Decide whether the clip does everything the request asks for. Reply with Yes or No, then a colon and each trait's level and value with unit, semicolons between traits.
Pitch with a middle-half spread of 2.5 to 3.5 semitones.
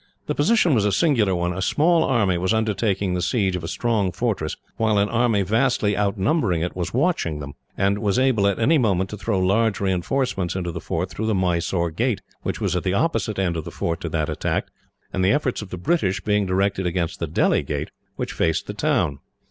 No: average, 4.0 semitones